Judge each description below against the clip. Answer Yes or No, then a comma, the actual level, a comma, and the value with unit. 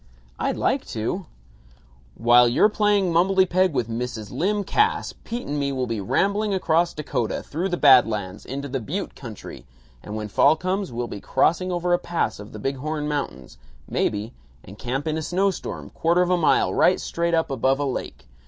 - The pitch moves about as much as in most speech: No, wide, 7.0 semitones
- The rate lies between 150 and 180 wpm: No, average, 195 wpm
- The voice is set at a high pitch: No, medium, 150 Hz